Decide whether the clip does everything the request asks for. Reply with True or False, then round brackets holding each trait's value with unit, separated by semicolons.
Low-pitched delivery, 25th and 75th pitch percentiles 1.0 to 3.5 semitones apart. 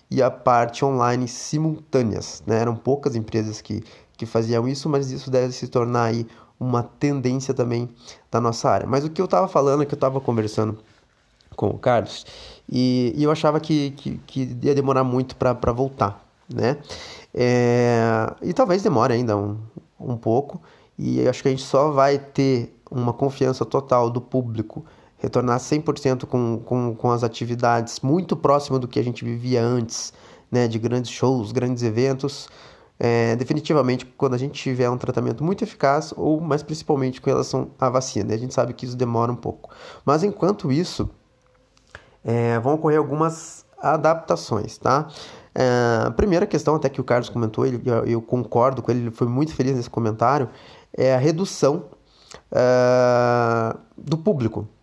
True (125 Hz; 2.8 semitones)